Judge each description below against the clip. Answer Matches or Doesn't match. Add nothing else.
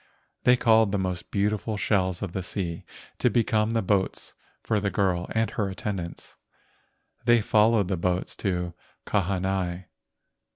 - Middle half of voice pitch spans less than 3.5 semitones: Matches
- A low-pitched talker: Matches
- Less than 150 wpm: Matches